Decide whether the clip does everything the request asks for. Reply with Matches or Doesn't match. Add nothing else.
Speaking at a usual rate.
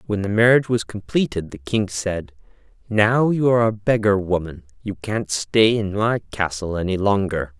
Matches